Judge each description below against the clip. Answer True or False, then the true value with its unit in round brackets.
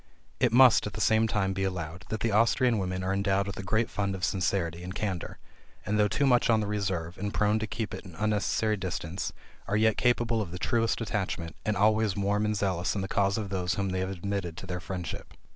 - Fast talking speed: True (235 wpm)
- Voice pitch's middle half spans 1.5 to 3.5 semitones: True (2.6 semitones)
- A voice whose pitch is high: False (100 Hz)